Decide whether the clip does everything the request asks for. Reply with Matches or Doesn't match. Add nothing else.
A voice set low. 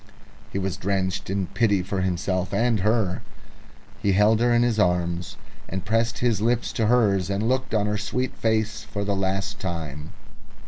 Matches